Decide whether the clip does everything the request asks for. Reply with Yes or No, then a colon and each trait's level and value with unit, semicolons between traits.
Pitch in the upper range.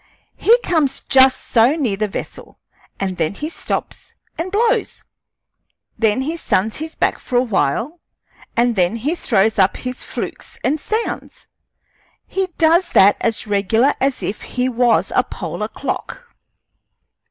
Yes: very high, 250 Hz